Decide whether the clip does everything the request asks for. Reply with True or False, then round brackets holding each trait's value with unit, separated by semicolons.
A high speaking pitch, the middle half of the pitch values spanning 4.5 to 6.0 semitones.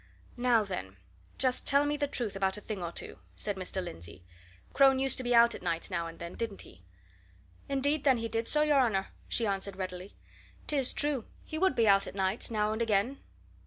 True (225 Hz; 5.6 semitones)